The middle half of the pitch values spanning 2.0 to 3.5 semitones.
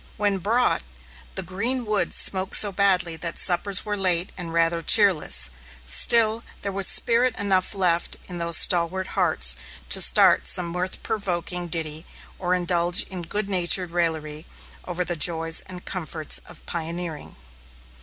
Yes: average, 2.7 semitones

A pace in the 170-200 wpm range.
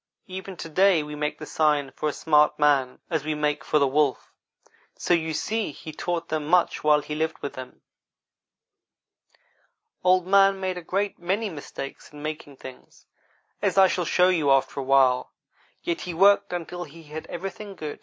Yes: average, 185 wpm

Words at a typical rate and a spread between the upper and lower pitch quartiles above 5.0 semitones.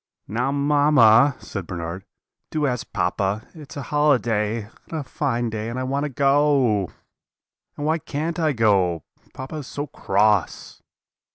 Yes: average, 150 wpm; wide, 5.4 semitones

